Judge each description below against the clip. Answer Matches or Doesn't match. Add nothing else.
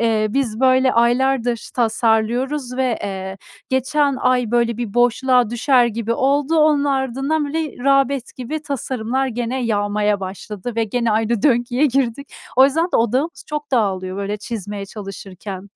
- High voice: Matches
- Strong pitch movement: Doesn't match